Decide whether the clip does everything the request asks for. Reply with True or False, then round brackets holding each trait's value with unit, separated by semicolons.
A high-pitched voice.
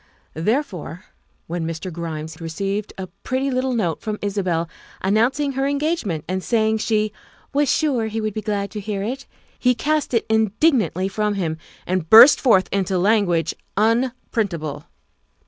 True (210 Hz)